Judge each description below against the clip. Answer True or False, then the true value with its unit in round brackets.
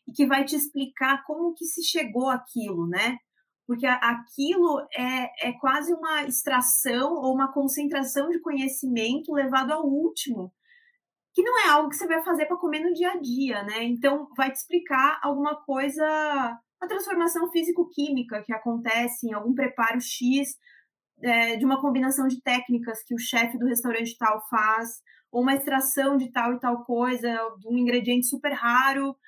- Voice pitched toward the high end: True (265 Hz)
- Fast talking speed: False (170 wpm)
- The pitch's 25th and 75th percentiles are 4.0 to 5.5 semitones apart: False (3.6 semitones)